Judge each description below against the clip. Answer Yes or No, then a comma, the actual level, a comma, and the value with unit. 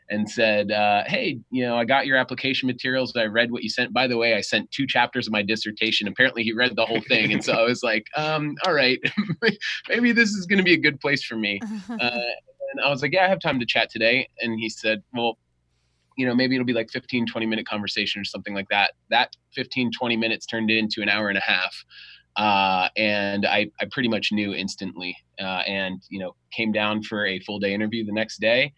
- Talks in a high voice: No, low, 115 Hz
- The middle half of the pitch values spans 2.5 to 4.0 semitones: Yes, average, 3.6 semitones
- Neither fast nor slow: No, fast, 240 wpm